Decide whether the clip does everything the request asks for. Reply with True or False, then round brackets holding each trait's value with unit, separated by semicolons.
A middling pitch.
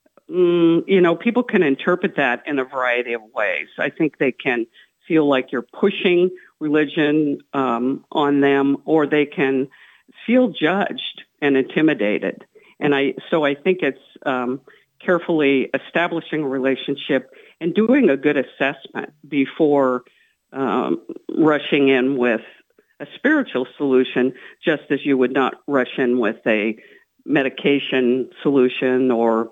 True (145 Hz)